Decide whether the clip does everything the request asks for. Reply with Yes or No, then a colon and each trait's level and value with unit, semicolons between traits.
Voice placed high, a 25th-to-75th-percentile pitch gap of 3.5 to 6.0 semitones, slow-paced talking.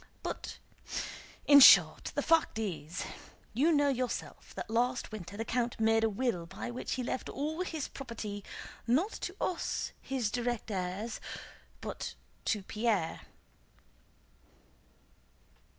Yes: high, 235 Hz; average, 4.1 semitones; slow, 125 wpm